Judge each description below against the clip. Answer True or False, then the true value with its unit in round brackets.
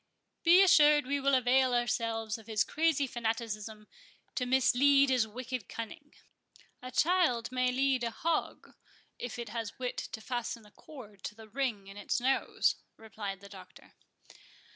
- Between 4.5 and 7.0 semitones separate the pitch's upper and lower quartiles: False (3.5 semitones)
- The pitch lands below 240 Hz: False (245 Hz)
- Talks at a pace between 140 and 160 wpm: True (150 wpm)